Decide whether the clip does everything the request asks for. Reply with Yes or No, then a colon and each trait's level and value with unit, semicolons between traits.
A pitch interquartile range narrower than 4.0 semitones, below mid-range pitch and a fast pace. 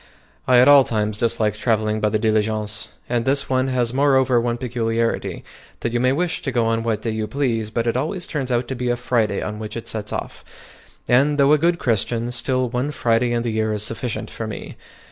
Yes: average, 2.7 semitones; low, 120 Hz; fast, 220 wpm